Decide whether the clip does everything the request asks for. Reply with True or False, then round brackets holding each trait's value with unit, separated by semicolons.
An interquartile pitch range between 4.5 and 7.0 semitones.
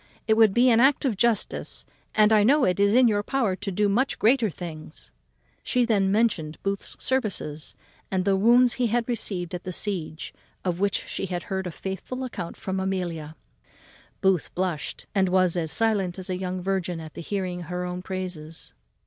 False (3.7 semitones)